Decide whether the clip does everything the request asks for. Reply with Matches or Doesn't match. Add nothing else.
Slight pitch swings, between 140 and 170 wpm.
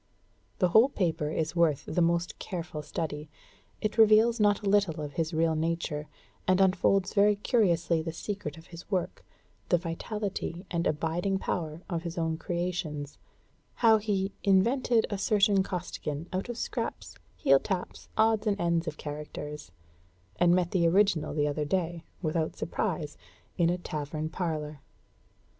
Doesn't match